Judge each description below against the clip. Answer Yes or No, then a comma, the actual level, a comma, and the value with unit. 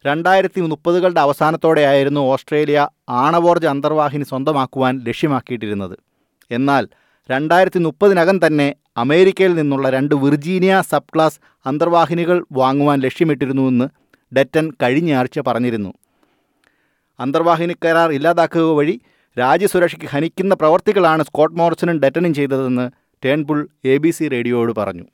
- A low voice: No, medium, 150 Hz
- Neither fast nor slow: Yes, average, 95 wpm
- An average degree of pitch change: Yes, average, 4.0 semitones